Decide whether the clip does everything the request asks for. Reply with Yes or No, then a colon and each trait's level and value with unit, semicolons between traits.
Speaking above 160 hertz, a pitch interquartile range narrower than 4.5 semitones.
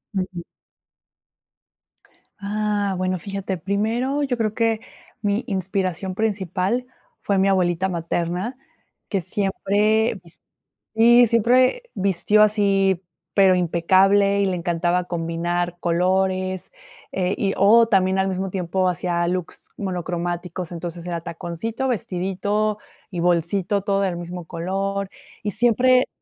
Yes: high, 190 Hz; average, 2.8 semitones